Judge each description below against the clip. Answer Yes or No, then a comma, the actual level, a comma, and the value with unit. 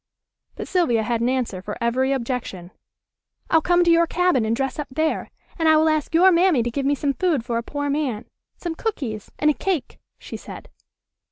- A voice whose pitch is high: Yes, very high, 280 Hz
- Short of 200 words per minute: No, fast, 205 wpm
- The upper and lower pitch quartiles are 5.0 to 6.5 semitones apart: Yes, wide, 5.6 semitones